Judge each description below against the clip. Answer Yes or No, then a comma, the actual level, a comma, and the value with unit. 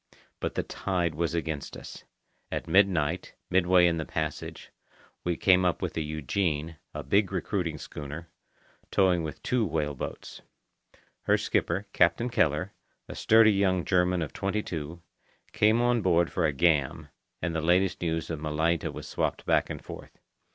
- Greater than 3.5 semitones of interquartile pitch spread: No, average, 3.0 semitones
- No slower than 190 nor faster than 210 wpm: No, average, 160 wpm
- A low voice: Yes, very low, 85 Hz